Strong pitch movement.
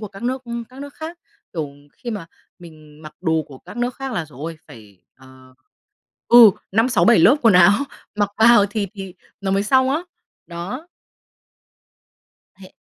Yes: wide, 7.0 semitones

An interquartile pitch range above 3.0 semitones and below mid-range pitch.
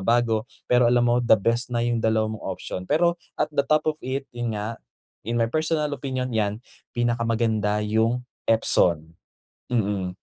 No: narrow, 2.5 semitones; low, 120 Hz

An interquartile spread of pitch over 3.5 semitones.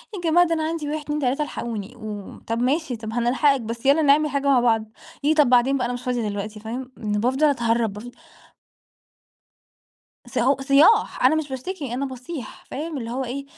Yes: average, 4.0 semitones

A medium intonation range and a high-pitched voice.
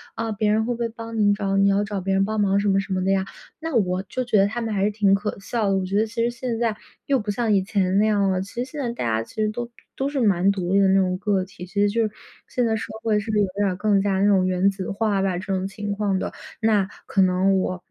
No: narrow, 2.3 semitones; high, 200 Hz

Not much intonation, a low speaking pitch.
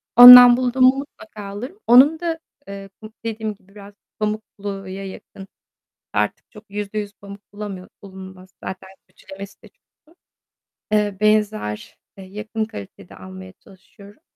No: narrow, 2.2 semitones; high, 205 Hz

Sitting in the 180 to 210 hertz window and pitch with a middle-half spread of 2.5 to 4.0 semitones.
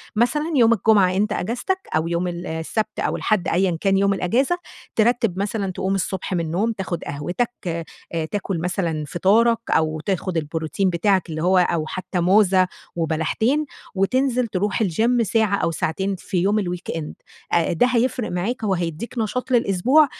No: high, 190 Hz; average, 4.6 semitones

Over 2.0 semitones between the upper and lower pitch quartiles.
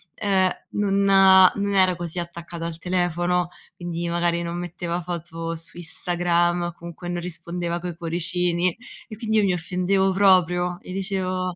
No: narrow, 1.5 semitones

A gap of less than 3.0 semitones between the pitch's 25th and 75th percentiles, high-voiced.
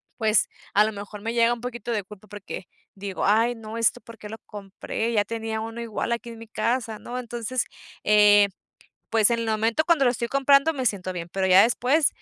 Yes: narrow, 2.4 semitones; high, 225 Hz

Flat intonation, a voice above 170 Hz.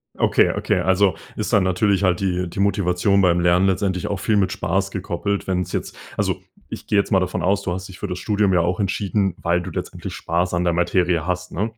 No: narrow, 1.9 semitones; very low, 95 Hz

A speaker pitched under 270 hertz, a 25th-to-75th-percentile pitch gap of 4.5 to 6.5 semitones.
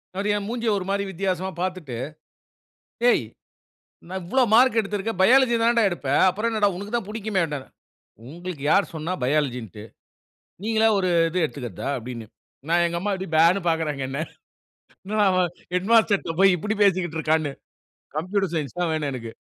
Yes: medium, 185 Hz; average, 4.8 semitones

